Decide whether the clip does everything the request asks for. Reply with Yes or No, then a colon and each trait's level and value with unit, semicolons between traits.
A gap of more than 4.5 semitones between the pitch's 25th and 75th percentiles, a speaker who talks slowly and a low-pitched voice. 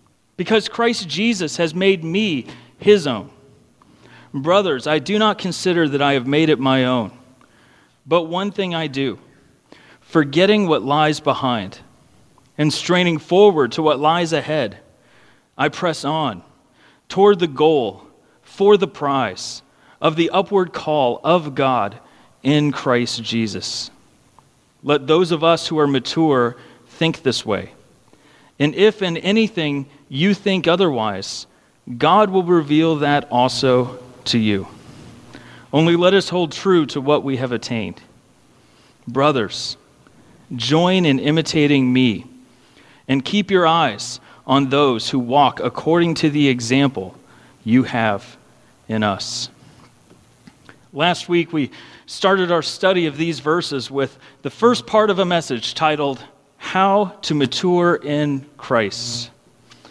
No: average, 5.2 semitones; slow, 130 wpm; medium, 150 Hz